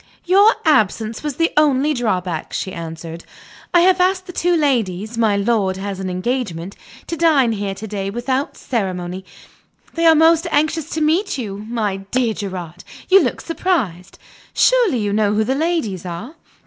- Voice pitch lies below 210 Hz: No, high, 230 Hz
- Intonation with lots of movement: Yes, wide, 8.5 semitones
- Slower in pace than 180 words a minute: Yes, average, 165 wpm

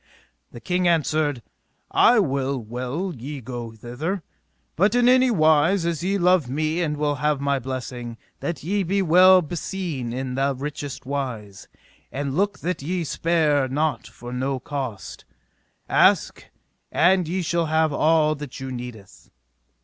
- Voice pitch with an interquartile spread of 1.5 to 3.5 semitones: No, average, 4.9 semitones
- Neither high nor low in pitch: Yes, medium, 150 Hz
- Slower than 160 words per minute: Yes, average, 150 wpm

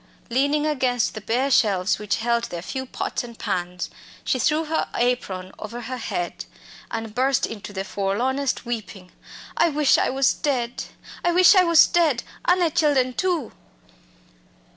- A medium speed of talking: Yes, average, 160 wpm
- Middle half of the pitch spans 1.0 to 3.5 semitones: No, average, 5.3 semitones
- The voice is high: Yes, very high, 250 Hz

